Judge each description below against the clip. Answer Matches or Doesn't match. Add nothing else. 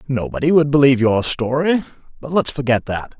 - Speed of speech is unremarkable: Matches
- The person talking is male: Matches